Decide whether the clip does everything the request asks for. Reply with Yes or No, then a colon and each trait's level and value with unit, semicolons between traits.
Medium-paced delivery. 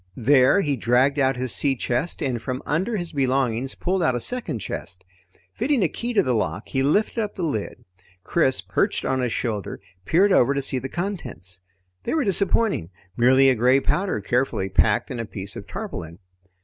Yes: average, 190 wpm